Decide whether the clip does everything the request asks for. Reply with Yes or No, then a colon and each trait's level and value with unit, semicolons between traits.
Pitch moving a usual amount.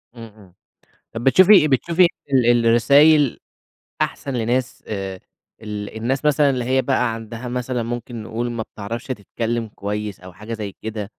Yes: average, 3.2 semitones